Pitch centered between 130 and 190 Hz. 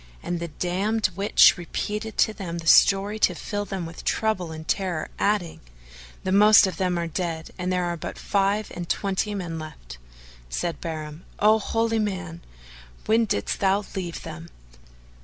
Yes: medium, 185 Hz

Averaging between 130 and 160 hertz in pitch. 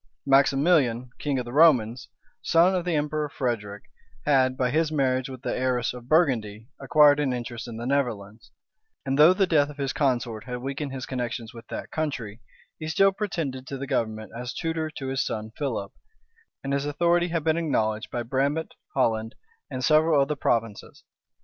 Yes: low, 135 Hz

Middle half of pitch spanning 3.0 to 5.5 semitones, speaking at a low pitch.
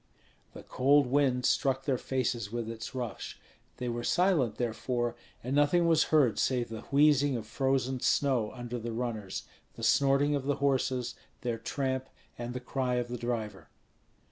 No: narrow, 2.5 semitones; low, 125 Hz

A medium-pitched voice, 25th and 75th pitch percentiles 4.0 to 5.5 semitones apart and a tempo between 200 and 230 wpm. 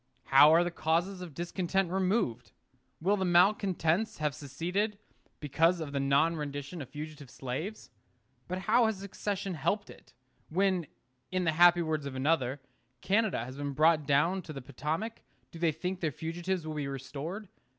No: medium, 165 Hz; average, 4.5 semitones; average, 165 wpm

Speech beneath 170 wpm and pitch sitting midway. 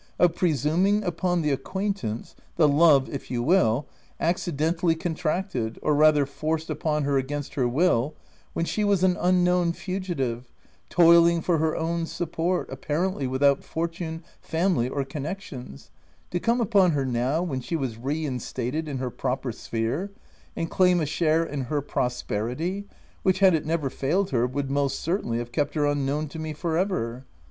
No: average, 175 wpm; medium, 155 Hz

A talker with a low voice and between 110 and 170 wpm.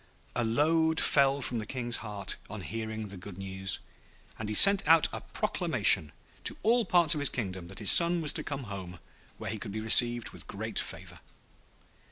No: low, 115 Hz; average, 195 wpm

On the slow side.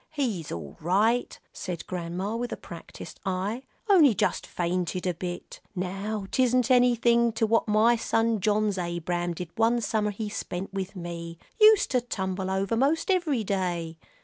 No: average, 155 wpm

